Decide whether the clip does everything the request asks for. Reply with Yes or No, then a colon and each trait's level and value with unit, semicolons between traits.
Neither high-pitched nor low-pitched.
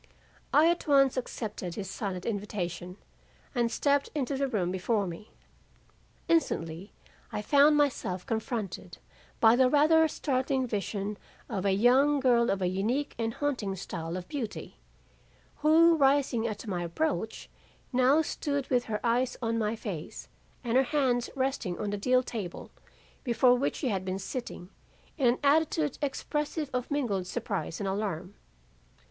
No: high, 235 Hz